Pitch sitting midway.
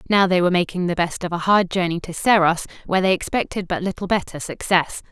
Yes: medium, 180 Hz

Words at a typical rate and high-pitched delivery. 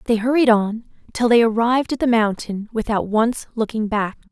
Yes: average, 180 wpm; high, 225 Hz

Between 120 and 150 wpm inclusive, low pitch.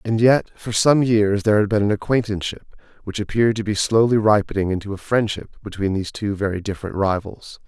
No: average, 195 wpm; low, 105 Hz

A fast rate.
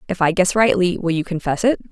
Yes: fast, 250 wpm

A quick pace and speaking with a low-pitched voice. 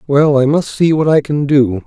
No: fast, 255 wpm; medium, 145 Hz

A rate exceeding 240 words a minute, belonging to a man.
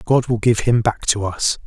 Yes: fast, 250 wpm; male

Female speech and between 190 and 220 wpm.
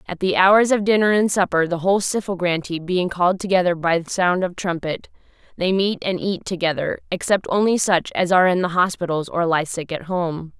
Yes: female; average, 200 wpm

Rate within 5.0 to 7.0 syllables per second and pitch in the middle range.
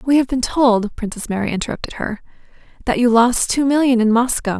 No: 5.7 syllables/s; high, 240 Hz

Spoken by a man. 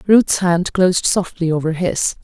No: female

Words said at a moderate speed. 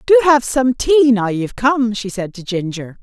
No: fast, 220 wpm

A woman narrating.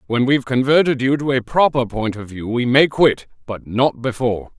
No: male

